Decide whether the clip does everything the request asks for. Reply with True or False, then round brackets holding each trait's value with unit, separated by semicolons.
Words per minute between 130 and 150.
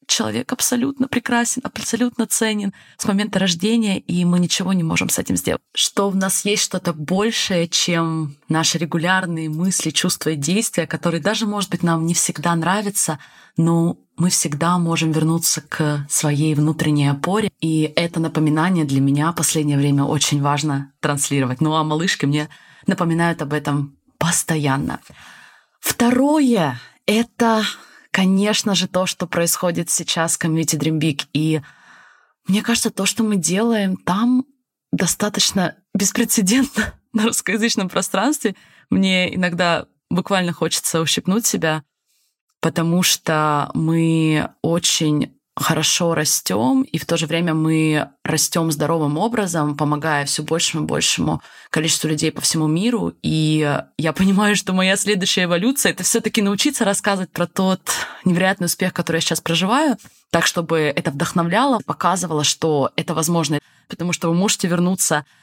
True (140 wpm)